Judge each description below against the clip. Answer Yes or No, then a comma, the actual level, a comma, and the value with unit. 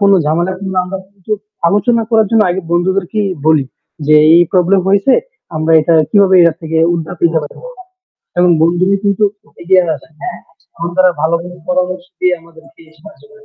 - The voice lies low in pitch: No, medium, 180 Hz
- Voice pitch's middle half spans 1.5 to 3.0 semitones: Yes, average, 2.7 semitones